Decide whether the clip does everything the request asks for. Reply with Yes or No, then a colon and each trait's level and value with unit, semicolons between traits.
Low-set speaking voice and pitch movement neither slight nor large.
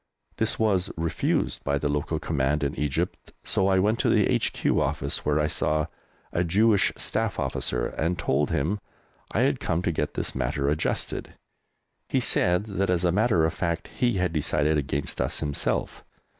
Yes: very low, 80 Hz; average, 4.1 semitones